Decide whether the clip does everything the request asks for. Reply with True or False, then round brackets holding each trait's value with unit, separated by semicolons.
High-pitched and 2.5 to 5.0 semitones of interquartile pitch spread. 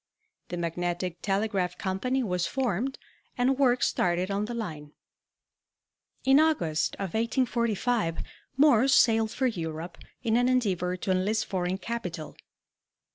False (205 Hz; 5.6 semitones)